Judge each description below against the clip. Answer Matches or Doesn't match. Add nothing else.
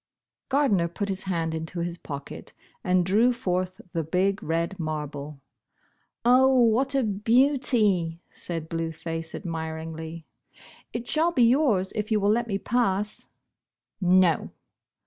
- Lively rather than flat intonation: Matches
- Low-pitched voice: Doesn't match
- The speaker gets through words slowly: Doesn't match